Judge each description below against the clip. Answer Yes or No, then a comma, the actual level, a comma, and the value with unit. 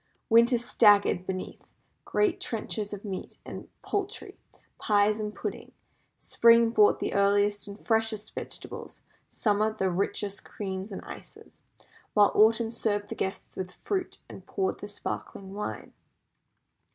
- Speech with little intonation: Yes, narrow, 2.2 semitones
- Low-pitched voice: No, high, 210 Hz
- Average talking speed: No, slow, 130 wpm